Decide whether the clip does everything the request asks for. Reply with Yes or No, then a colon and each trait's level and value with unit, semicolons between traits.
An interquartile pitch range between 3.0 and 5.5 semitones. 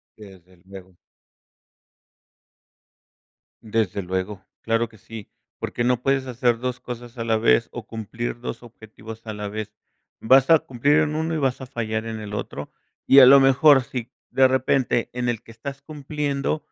Yes: average, 3.5 semitones